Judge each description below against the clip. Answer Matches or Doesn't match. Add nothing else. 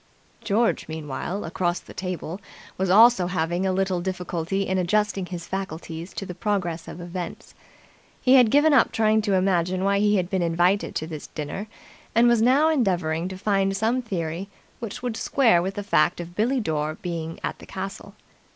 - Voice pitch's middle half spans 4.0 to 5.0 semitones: Doesn't match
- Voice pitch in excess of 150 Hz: Matches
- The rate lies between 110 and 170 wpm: Doesn't match